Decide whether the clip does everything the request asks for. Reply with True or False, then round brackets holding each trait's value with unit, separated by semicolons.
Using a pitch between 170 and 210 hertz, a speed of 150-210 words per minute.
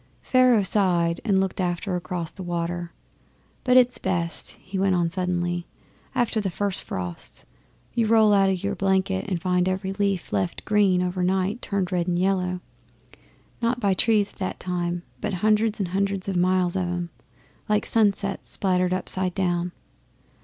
True (185 Hz; 160 wpm)